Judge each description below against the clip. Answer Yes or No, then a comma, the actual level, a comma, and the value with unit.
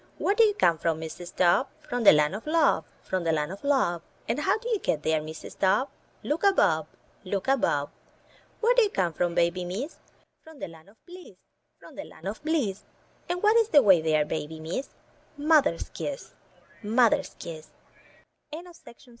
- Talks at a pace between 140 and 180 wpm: No, average, 190 wpm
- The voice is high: Yes, high, 200 Hz